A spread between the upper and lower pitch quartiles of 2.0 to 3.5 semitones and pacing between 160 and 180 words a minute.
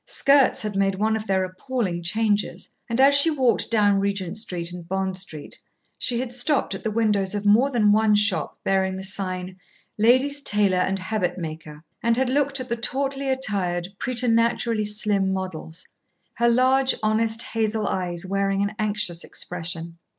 No: average, 4.0 semitones; average, 165 wpm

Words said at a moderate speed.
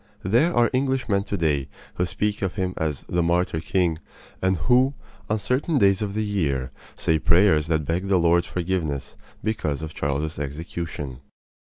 Yes: average, 165 wpm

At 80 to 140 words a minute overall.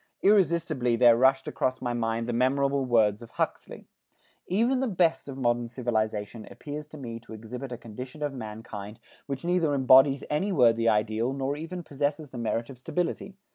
No: average, 175 wpm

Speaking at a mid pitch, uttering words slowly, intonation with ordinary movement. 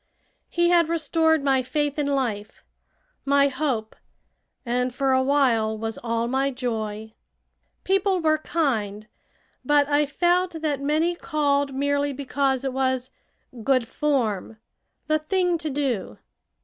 No: very high, 280 Hz; slow, 130 wpm; average, 3.6 semitones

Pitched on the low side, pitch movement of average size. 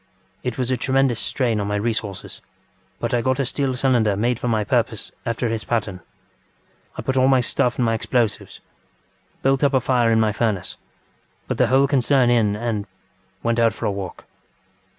Yes: low, 120 Hz; average, 3.3 semitones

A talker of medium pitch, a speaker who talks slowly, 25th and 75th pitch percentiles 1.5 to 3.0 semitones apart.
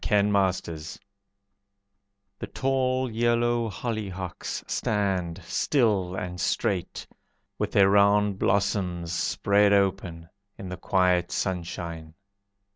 No: very low, 95 Hz; slow, 90 wpm; narrow, 2.6 semitones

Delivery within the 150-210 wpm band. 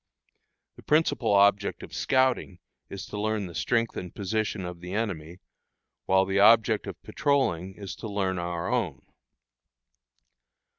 No: average, 140 wpm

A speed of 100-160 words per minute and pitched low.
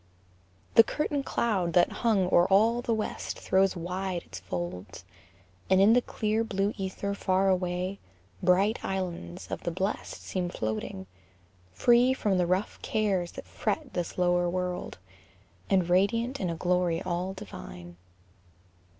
No: average, 140 wpm; medium, 185 Hz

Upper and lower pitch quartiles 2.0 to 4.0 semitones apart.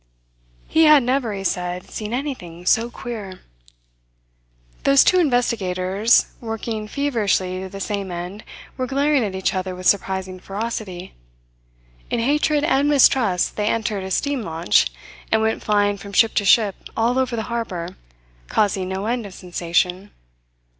No: average, 4.5 semitones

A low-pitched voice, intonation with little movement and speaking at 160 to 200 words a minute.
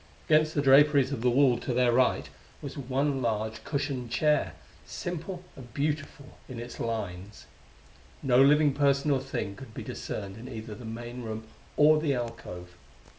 No: low, 130 Hz; average, 3.8 semitones; average, 165 wpm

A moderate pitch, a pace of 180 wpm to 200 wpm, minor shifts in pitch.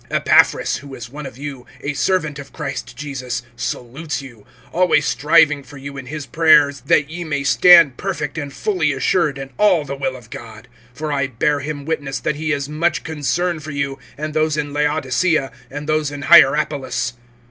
Yes: medium, 145 Hz; average, 185 wpm; narrow, 2.3 semitones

